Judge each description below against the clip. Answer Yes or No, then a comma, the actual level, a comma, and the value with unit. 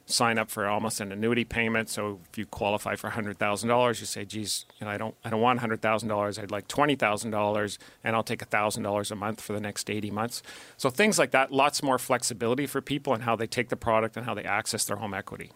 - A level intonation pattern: Yes, narrow, 2.2 semitones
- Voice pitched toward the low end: Yes, low, 110 Hz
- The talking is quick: Yes, fast, 230 wpm